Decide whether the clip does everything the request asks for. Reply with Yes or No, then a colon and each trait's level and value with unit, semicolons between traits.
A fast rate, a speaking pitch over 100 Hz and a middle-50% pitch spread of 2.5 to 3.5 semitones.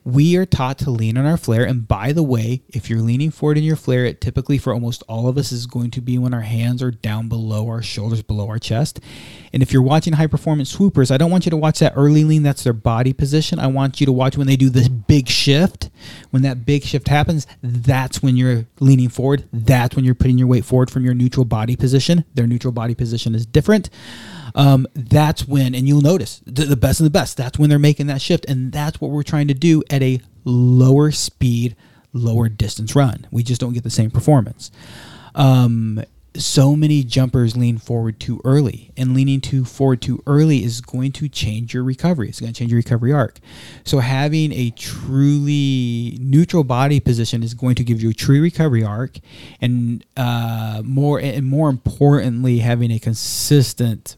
Yes: fast, 210 wpm; low, 130 Hz; average, 3.2 semitones